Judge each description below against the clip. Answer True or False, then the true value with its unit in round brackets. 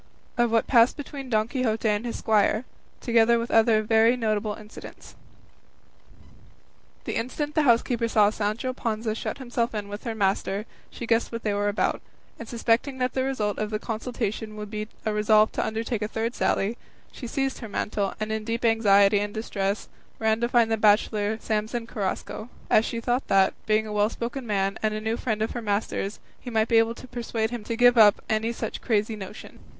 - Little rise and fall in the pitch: True (1.9 semitones)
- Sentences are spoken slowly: False (195 wpm)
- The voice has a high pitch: True (220 Hz)